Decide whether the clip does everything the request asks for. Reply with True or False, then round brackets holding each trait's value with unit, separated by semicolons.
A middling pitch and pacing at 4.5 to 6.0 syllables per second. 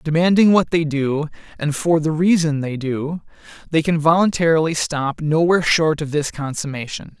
True (155 Hz; 4.9 syllables/s)